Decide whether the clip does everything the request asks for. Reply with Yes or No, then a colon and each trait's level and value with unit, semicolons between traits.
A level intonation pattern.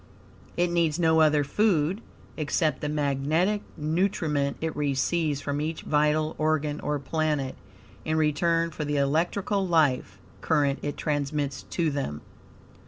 Yes: narrow, 2.3 semitones